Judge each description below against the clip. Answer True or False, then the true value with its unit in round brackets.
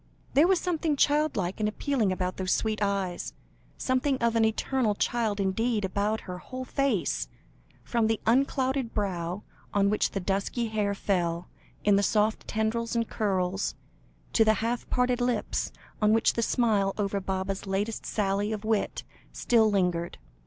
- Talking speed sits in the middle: True (155 wpm)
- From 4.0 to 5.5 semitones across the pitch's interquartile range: False (3.3 semitones)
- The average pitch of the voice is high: True (215 Hz)